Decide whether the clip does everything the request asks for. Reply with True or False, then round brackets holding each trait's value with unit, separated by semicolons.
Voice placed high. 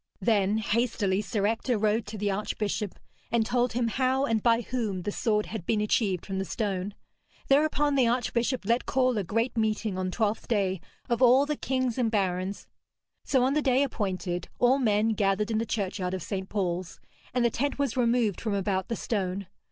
True (220 Hz)